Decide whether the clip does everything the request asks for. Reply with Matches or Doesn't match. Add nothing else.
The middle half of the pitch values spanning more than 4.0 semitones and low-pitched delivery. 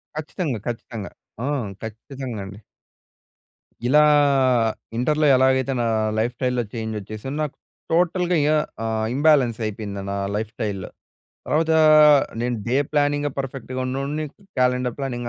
Matches